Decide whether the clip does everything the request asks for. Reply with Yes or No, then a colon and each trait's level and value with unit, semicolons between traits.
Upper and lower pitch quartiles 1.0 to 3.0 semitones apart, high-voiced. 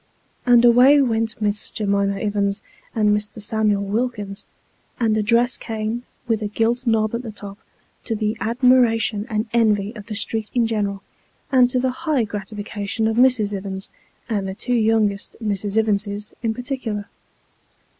Yes: narrow, 2.4 semitones; high, 220 Hz